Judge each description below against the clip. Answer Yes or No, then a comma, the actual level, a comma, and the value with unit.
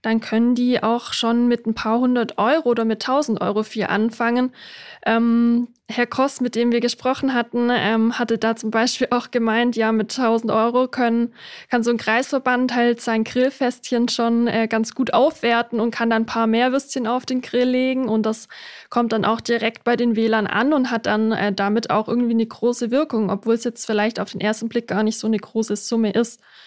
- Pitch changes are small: Yes, narrow, 1.6 semitones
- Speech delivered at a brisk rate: Yes, fast, 210 wpm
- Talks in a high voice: Yes, high, 235 Hz